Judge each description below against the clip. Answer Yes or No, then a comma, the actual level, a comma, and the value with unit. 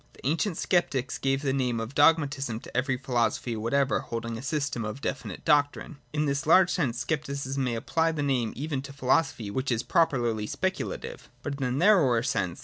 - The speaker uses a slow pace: No, average, 190 wpm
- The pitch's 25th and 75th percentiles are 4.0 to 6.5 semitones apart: No, average, 3.5 semitones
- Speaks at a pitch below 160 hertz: Yes, low, 135 Hz